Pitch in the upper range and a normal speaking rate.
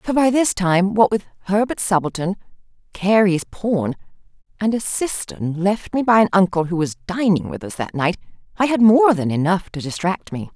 Yes: high, 195 Hz; average, 190 wpm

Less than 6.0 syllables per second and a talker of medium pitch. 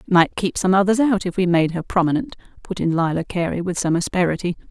No: 6.2 syllables/s; medium, 180 Hz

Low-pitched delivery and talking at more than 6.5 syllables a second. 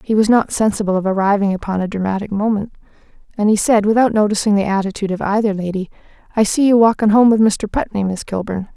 No: high, 205 Hz; 6.7 syllables/s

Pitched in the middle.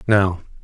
No: very low, 95 Hz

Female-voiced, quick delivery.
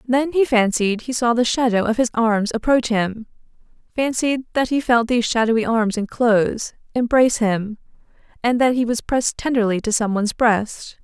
No: female; average, 165 wpm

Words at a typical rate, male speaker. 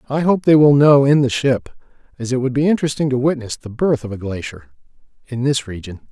No: fast, 225 wpm; male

